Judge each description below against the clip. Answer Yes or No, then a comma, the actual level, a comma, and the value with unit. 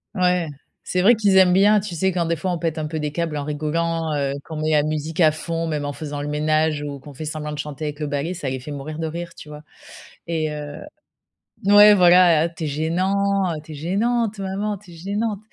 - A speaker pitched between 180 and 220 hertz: No, medium, 160 Hz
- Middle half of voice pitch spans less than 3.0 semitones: No, average, 3.5 semitones